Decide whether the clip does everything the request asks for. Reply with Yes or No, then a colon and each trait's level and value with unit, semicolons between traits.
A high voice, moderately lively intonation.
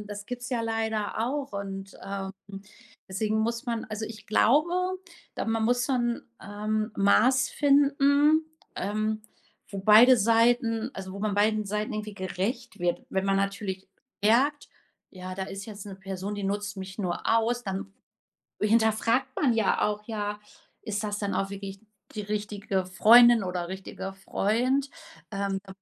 Yes: high, 215 Hz; average, 3.0 semitones